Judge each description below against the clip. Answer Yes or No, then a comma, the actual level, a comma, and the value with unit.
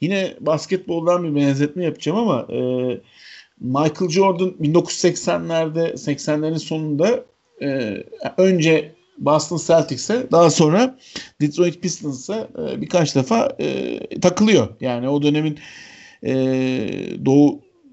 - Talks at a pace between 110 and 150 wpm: No, average, 100 wpm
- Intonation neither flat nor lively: Yes, average, 4.1 semitones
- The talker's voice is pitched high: No, medium, 160 Hz